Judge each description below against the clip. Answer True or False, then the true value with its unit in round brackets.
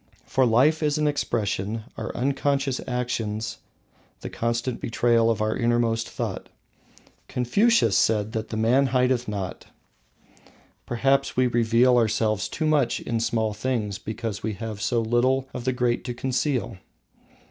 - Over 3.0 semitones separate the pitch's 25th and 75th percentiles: False (2.7 semitones)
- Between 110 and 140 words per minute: True (135 wpm)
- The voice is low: True (120 Hz)